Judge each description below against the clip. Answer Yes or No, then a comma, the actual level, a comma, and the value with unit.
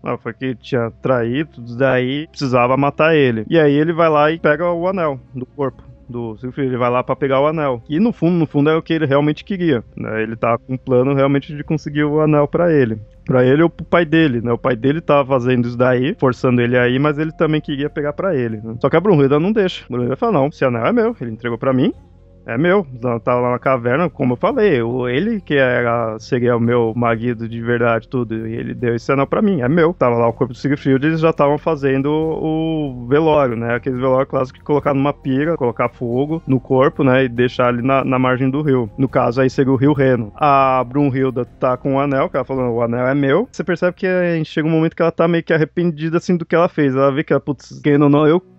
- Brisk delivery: Yes, fast, 255 wpm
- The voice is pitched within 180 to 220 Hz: No, low, 135 Hz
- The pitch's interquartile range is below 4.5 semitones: Yes, average, 4.1 semitones